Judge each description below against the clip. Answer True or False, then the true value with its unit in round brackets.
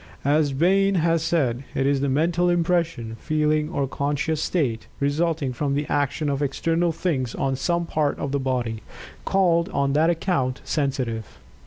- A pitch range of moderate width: True (3.6 semitones)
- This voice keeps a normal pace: True (160 wpm)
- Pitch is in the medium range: True (150 Hz)